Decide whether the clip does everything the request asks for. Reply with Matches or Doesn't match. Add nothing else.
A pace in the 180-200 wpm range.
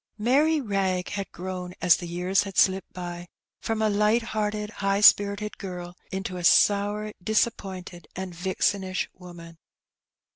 Doesn't match